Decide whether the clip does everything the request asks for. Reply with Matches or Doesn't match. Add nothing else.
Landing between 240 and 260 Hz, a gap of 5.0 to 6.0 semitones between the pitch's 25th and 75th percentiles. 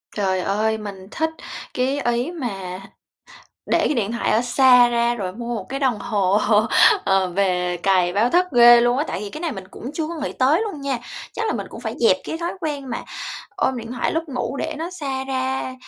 Matches